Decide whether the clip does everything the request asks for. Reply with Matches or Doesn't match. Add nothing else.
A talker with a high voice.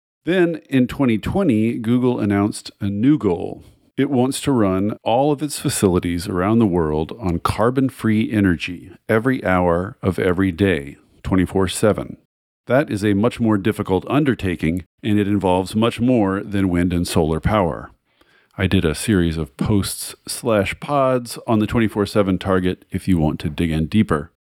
Doesn't match